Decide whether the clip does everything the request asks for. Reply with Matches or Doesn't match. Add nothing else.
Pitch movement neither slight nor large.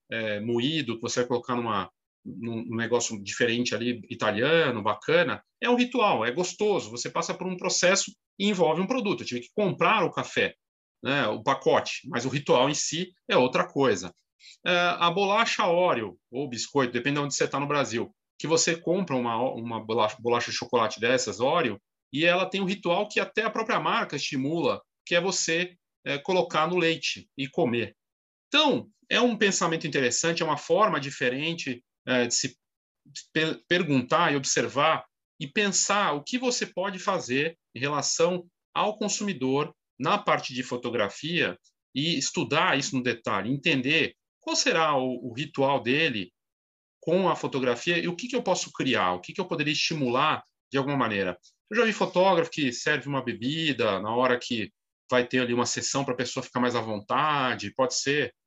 Doesn't match